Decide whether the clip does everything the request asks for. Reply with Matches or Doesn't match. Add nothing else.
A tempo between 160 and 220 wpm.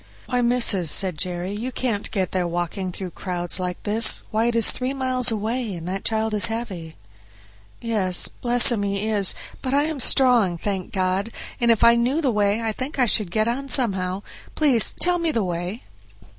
Matches